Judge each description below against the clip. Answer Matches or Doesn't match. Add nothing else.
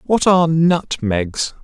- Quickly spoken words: Doesn't match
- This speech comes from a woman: Doesn't match